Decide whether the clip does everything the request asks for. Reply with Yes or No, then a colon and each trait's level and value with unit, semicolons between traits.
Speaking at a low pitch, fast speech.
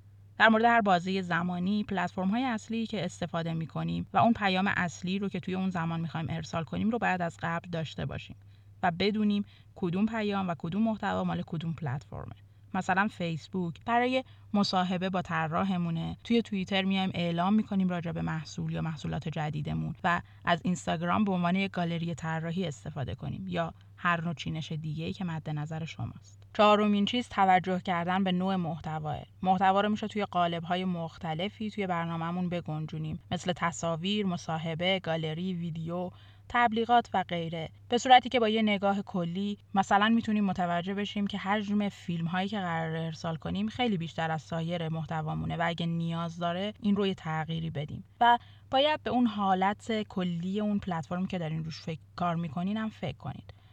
No: medium, 175 Hz; fast, 170 wpm